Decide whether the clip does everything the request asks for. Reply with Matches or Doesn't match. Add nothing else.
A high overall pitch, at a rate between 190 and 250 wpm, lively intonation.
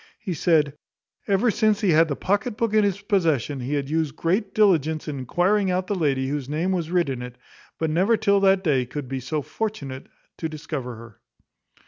Doesn't match